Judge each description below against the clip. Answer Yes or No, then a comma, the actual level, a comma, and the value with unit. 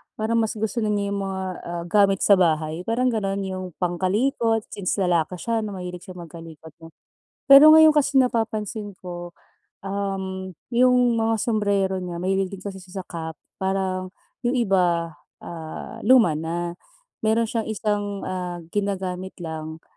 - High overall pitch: Yes, high, 195 Hz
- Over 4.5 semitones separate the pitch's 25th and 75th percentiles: No, average, 3.7 semitones